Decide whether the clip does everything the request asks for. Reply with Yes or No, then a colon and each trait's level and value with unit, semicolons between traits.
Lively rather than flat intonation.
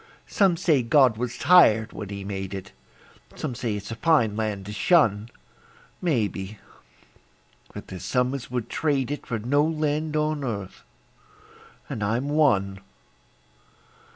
Yes: wide, 6.2 semitones